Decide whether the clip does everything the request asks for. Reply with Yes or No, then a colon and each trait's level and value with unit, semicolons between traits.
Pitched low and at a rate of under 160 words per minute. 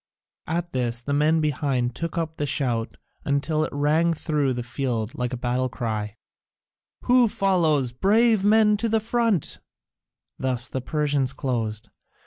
No: medium, 145 Hz; average, 145 wpm